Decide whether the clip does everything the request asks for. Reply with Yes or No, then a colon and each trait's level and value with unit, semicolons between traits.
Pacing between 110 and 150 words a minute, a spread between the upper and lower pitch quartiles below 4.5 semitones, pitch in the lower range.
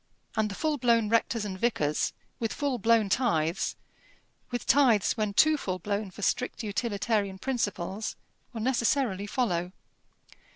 No: slow, 135 wpm; average, 3.5 semitones; high, 220 Hz